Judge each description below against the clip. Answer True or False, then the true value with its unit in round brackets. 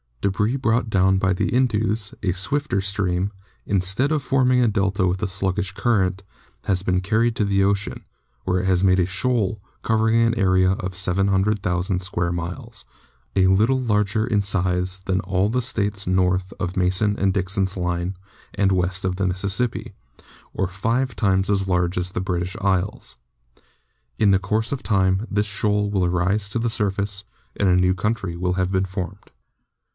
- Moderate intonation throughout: False (2.2 semitones)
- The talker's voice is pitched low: True (95 Hz)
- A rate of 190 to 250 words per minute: False (170 wpm)